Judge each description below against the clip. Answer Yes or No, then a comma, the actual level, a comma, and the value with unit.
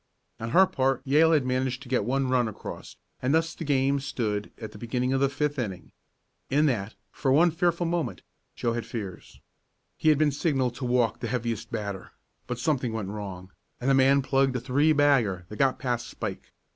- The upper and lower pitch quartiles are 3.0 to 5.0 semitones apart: Yes, average, 3.6 semitones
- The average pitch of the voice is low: Yes, low, 130 Hz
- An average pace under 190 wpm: No, average, 200 wpm